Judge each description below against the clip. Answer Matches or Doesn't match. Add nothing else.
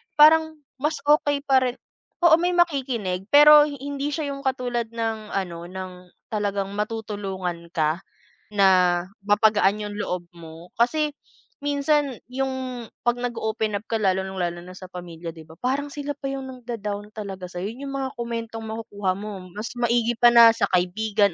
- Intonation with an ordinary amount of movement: Doesn't match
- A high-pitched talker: Matches